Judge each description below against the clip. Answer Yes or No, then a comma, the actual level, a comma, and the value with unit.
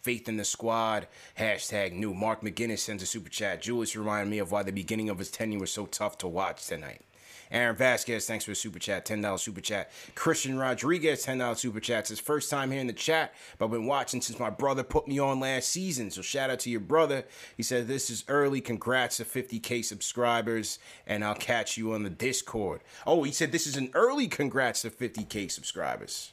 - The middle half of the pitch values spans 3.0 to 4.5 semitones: Yes, average, 3.8 semitones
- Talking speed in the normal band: No, fast, 220 wpm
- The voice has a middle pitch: No, low, 115 Hz